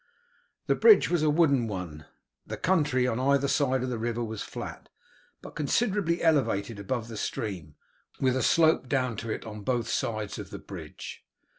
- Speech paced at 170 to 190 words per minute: Yes, average, 175 wpm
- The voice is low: Yes, low, 125 Hz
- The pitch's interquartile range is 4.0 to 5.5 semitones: Yes, average, 5.0 semitones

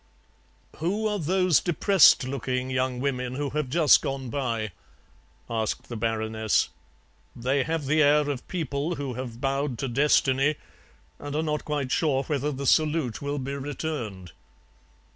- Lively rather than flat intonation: No, average, 3.0 semitones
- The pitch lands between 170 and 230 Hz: No, medium, 140 Hz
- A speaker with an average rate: Yes, average, 145 wpm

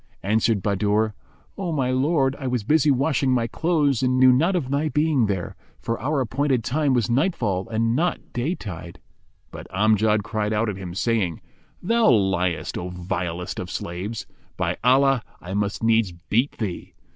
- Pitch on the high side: No, low, 115 Hz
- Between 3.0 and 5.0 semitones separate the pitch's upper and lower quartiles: No, wide, 5.4 semitones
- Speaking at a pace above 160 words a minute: Yes, average, 170 wpm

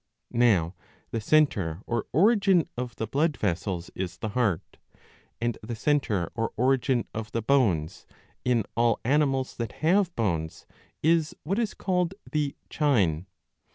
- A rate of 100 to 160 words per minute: Yes, average, 140 wpm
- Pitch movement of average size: No, wide, 6.8 semitones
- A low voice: Yes, low, 120 Hz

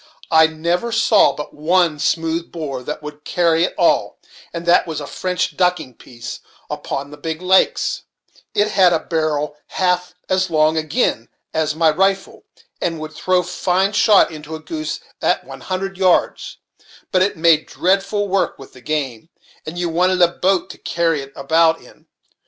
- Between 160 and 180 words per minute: Yes, average, 170 wpm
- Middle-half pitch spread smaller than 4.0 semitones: Yes, average, 3.0 semitones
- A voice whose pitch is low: No, medium, 170 Hz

